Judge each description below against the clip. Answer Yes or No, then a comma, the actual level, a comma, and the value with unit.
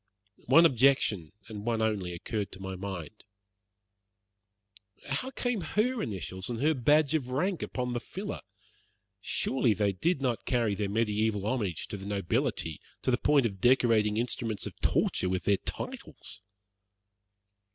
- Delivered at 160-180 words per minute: No, average, 145 wpm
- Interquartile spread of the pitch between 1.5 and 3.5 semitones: No, average, 5.2 semitones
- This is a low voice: Yes, low, 115 Hz